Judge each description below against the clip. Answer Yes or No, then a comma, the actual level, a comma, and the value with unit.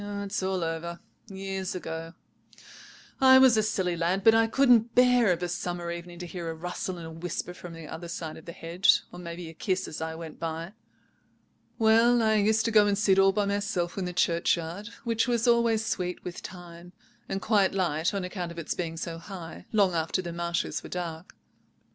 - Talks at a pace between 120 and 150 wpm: No, fast, 205 wpm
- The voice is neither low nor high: Yes, medium, 180 Hz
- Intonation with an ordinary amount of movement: Yes, average, 3.6 semitones